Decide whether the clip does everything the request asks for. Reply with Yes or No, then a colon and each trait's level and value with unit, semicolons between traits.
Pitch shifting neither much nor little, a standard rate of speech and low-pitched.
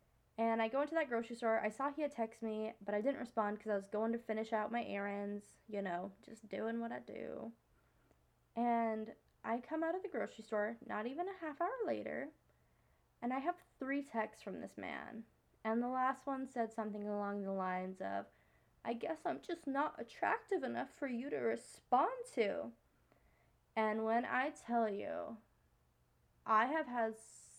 No: average, 3.9 semitones; average, 185 wpm; high, 225 Hz